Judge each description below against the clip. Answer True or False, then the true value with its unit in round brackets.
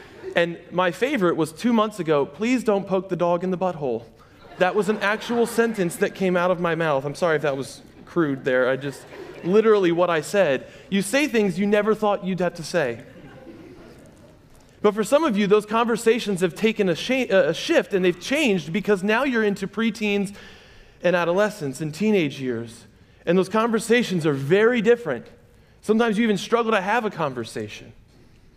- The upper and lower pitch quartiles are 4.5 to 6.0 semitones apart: True (4.8 semitones)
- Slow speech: False (185 wpm)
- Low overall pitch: False (190 Hz)